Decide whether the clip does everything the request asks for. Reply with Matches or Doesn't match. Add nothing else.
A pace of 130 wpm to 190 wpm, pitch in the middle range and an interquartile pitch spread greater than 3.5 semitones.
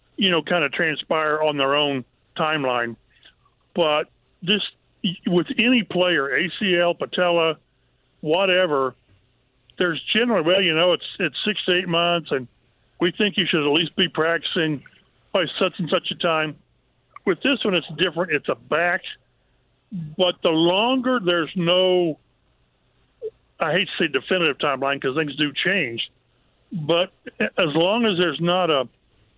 Matches